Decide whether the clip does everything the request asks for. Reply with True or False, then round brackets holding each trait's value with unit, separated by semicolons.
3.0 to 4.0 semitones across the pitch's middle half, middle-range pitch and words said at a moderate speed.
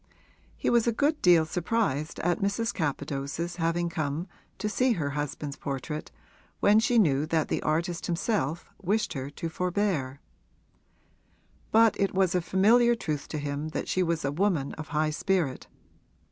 False (5.0 semitones; 170 Hz; 160 wpm)